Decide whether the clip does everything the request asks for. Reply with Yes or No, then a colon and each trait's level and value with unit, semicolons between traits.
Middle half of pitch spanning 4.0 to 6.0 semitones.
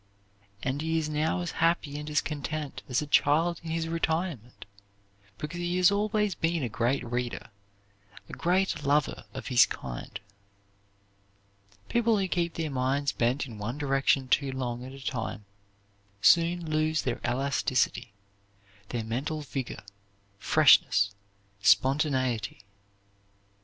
Yes: average, 4.6 semitones